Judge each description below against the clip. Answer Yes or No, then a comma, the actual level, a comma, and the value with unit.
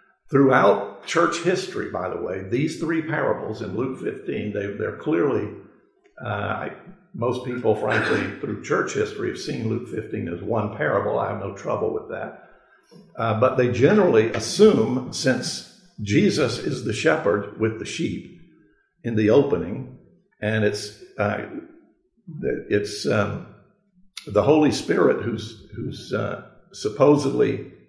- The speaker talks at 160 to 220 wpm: No, slow, 135 wpm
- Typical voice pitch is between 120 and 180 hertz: Yes, medium, 140 Hz